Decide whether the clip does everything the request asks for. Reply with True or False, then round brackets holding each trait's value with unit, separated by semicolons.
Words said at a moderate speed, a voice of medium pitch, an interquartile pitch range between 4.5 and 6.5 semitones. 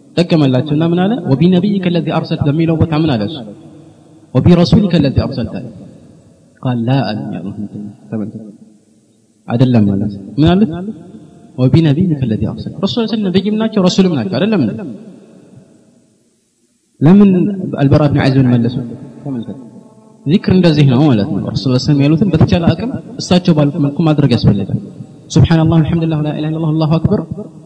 False (155 wpm; 150 Hz; 5.5 semitones)